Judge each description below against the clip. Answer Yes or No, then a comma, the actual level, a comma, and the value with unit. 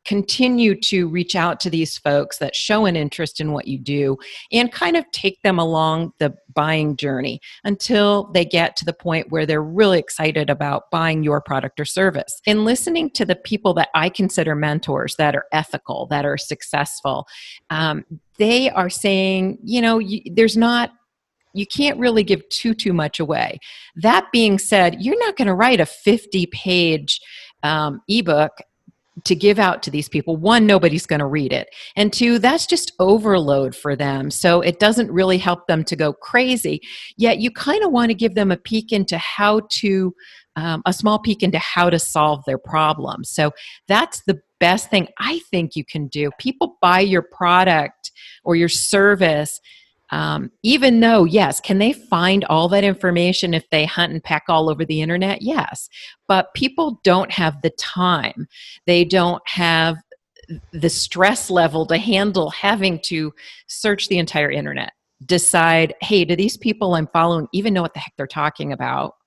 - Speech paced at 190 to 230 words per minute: No, average, 180 wpm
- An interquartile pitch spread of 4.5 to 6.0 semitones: Yes, average, 4.9 semitones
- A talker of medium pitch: Yes, medium, 180 Hz